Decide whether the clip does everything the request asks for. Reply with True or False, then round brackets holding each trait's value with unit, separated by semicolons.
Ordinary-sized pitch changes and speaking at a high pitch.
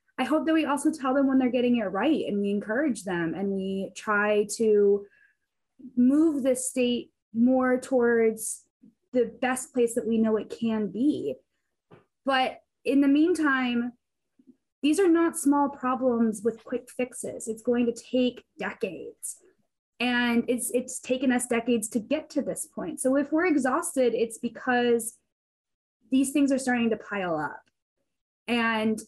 True (3.4 semitones; 250 Hz)